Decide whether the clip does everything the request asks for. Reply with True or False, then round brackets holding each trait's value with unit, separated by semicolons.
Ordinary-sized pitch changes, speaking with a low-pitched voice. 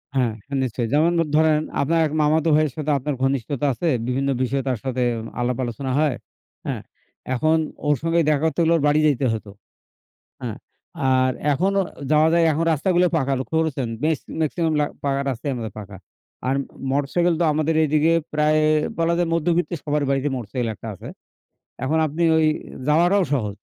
False (3.6 semitones; 150 Hz)